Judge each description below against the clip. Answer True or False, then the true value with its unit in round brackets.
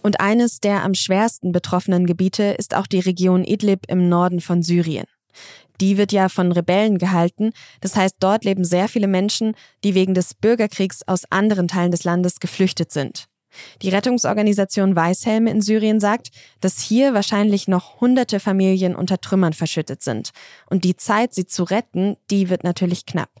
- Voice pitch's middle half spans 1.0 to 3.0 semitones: True (2.4 semitones)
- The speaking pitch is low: False (190 Hz)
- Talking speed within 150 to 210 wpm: True (170 wpm)